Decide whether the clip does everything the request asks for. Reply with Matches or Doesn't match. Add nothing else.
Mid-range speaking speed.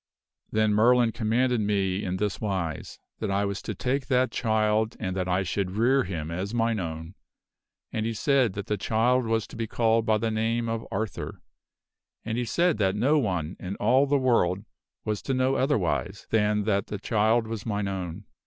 Matches